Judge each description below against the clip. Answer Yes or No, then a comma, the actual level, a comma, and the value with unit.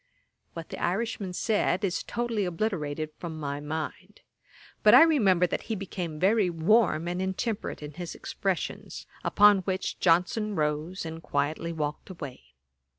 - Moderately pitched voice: Yes, medium, 180 Hz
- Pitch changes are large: No, average, 4.3 semitones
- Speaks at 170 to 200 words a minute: No, average, 145 wpm